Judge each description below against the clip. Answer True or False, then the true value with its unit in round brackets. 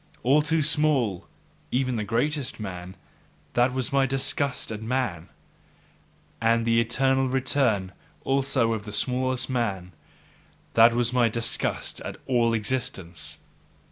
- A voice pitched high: False (120 Hz)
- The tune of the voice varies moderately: True (3.2 semitones)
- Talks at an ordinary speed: False (125 wpm)